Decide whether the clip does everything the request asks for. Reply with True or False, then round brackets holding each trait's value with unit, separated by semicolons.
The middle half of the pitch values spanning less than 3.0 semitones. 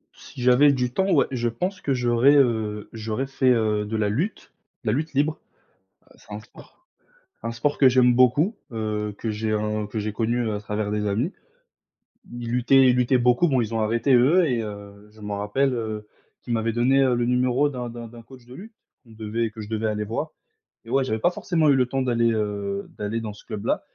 False (3.3 semitones)